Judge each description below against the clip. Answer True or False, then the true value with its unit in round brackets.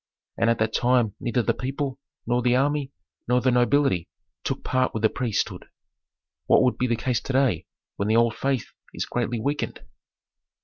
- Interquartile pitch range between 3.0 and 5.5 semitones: False (2.4 semitones)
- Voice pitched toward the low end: True (125 Hz)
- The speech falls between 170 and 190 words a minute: True (180 wpm)